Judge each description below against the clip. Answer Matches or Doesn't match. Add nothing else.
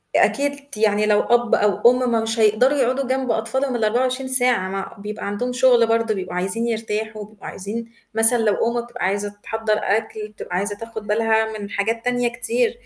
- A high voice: Matches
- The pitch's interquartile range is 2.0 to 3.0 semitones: Matches